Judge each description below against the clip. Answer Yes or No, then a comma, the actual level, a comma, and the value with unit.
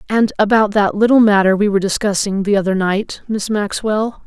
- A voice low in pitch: No, high, 205 Hz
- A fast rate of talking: No, average, 185 wpm